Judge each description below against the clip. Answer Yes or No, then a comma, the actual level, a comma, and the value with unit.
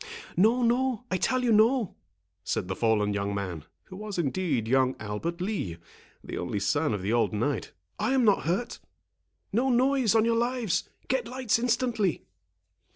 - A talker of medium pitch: No, high, 195 Hz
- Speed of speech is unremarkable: Yes, average, 160 wpm